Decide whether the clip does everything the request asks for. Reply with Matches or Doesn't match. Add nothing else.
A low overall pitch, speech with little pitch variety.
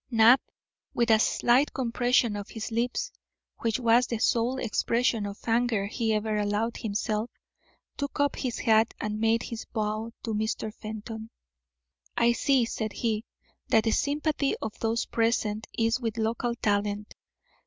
Doesn't match